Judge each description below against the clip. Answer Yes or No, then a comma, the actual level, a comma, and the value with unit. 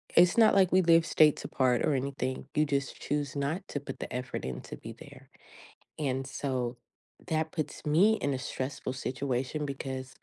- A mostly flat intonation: No, average, 3.1 semitones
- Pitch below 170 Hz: Yes, medium, 140 Hz